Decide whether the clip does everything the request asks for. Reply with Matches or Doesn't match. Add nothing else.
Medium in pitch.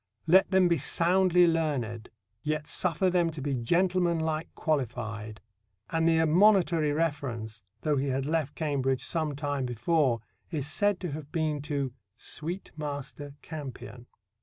Matches